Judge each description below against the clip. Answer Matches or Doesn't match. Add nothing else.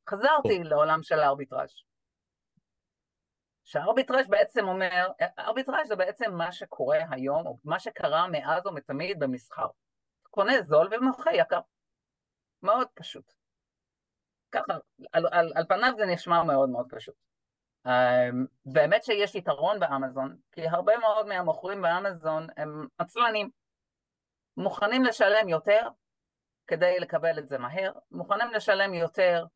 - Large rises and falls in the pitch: Matches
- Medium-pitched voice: Matches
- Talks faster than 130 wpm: Doesn't match